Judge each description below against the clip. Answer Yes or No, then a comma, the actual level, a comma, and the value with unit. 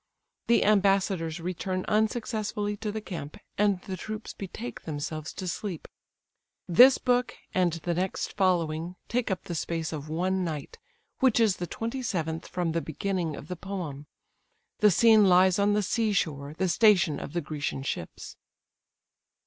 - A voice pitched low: No, medium, 185 Hz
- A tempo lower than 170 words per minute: Yes, average, 155 wpm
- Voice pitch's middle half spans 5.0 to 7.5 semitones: No, average, 4.3 semitones